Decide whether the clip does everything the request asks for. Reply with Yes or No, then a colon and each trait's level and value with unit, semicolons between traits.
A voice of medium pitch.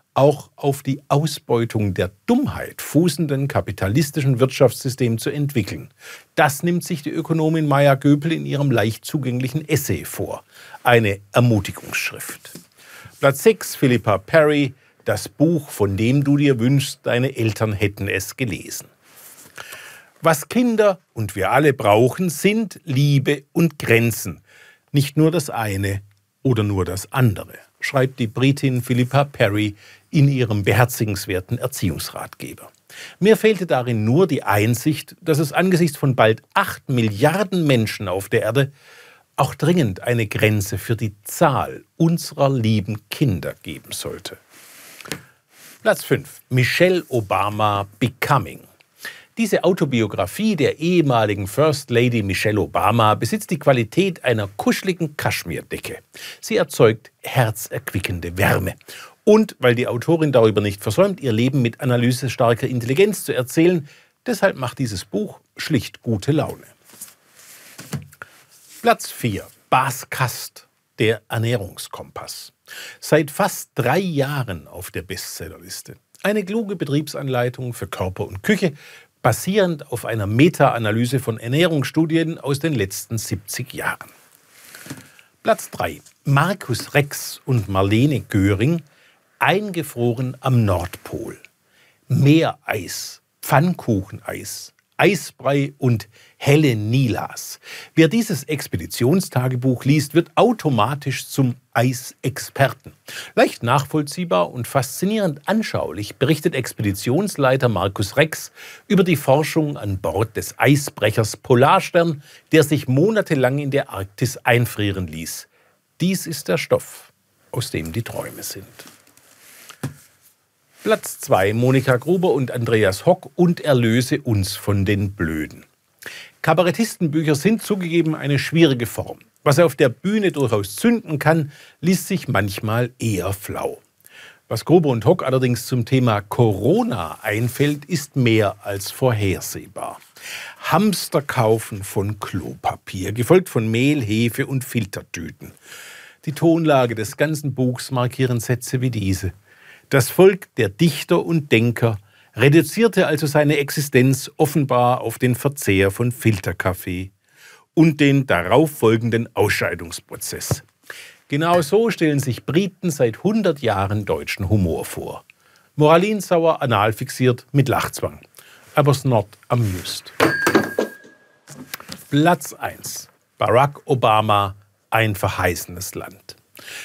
No: low, 130 Hz